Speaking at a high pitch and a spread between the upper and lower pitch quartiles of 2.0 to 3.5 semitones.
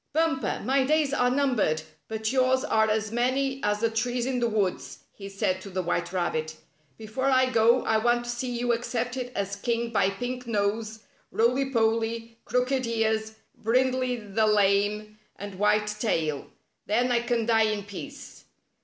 Yes: high, 230 Hz; average, 3.0 semitones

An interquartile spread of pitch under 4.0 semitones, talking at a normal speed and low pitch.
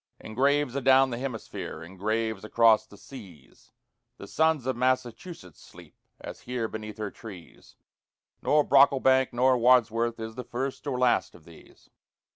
Yes: average, 3.3 semitones; average, 150 wpm; low, 120 Hz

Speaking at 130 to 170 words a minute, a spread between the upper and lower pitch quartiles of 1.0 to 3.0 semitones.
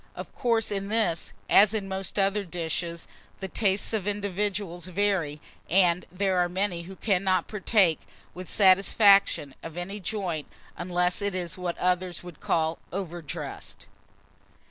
Yes: average, 140 wpm; narrow, 2.5 semitones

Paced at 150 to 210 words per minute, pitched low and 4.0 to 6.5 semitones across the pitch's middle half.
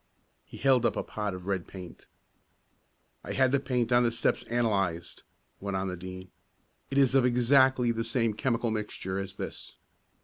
Yes: average, 175 wpm; low, 115 Hz; average, 4.5 semitones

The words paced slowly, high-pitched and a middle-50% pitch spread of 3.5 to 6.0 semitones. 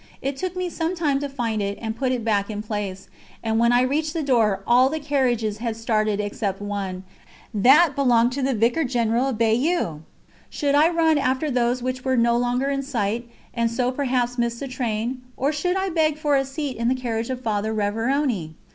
No: fast, 205 wpm; high, 245 Hz; average, 3.8 semitones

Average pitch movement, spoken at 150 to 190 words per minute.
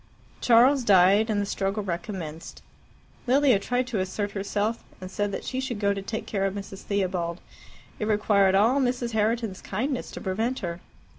Yes: average, 3.3 semitones; average, 170 wpm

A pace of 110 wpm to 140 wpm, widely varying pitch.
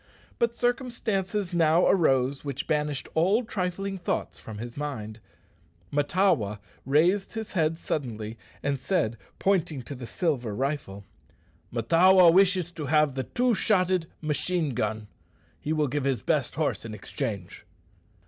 Yes: slow, 135 wpm; wide, 6.4 semitones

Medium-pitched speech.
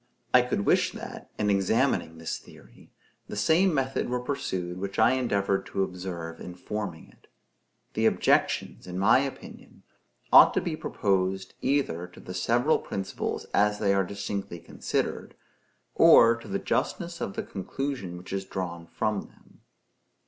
No: low, 100 Hz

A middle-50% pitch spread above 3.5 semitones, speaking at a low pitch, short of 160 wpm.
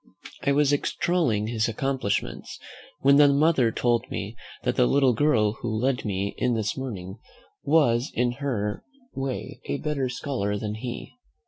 Yes: average, 4.5 semitones; low, 125 Hz; average, 150 wpm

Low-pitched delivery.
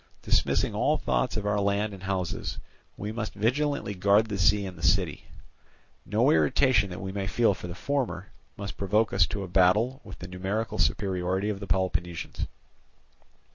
Yes: low, 100 Hz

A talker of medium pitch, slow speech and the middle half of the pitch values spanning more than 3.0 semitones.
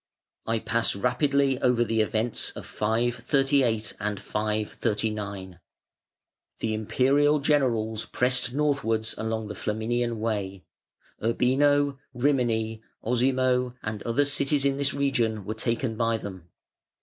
No: low, 115 Hz; slow, 115 wpm; average, 3.7 semitones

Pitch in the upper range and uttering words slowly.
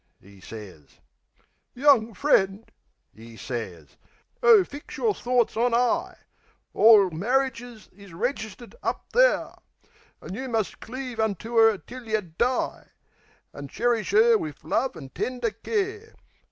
Yes: high, 230 Hz; slow, 125 wpm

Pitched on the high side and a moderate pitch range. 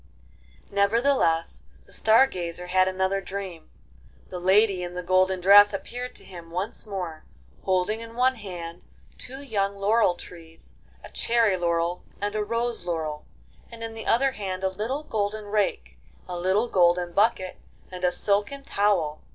Yes: high, 195 Hz; average, 3.7 semitones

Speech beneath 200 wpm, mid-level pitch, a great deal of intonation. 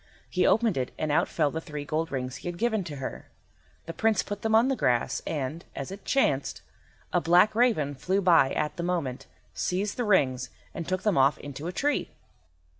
No: fast, 205 wpm; medium, 170 Hz; wide, 6.4 semitones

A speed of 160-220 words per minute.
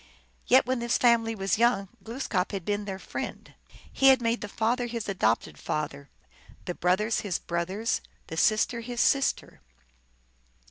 No: average, 150 wpm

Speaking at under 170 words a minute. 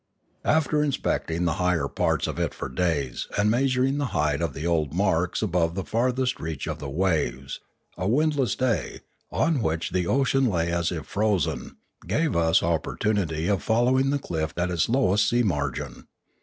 No: average, 175 wpm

